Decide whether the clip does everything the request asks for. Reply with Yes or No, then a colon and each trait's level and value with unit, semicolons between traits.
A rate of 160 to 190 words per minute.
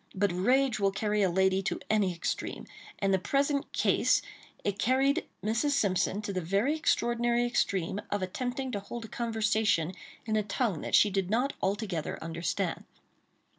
Yes: average, 170 wpm